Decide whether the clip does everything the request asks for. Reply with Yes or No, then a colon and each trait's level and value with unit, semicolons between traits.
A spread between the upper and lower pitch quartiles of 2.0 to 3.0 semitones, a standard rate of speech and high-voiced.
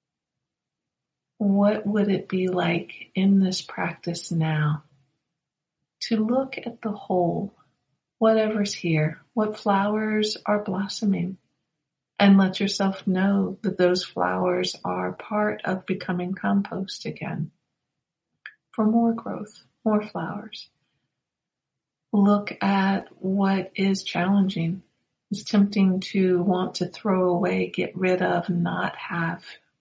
No: average, 2.7 semitones; slow, 110 wpm; high, 195 Hz